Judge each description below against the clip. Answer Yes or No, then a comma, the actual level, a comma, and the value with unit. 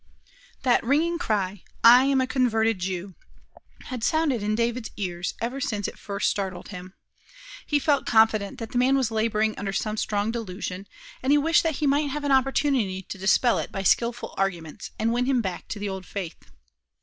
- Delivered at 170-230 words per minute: Yes, average, 190 wpm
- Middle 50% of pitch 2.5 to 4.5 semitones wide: No, average, 5.0 semitones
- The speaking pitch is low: No, high, 225 Hz